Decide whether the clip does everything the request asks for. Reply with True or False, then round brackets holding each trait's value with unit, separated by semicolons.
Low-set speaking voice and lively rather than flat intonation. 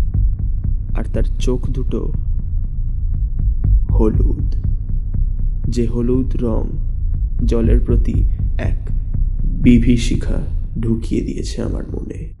False (100 Hz; 3.5 semitones)